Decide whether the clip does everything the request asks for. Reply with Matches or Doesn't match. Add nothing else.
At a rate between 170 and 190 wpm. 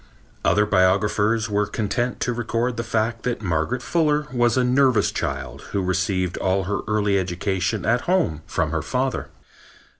Doesn't match